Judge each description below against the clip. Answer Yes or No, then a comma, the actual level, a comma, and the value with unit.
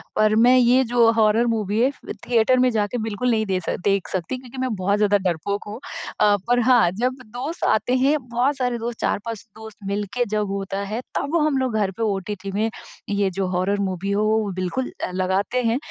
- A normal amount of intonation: Yes, average, 3.6 semitones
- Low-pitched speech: No, high, 220 Hz